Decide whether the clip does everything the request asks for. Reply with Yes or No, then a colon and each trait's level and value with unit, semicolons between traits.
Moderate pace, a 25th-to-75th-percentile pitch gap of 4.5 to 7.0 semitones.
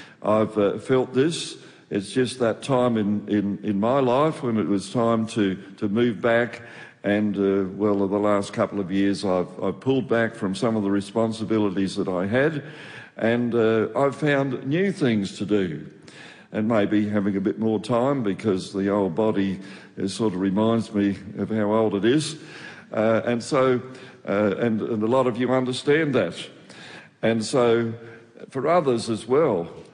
No: average, 175 wpm; average, 3.4 semitones